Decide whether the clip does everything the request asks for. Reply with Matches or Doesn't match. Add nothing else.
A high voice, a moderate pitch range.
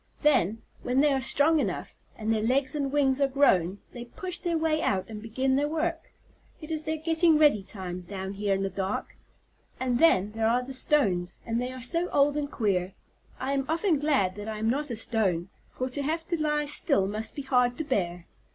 Doesn't match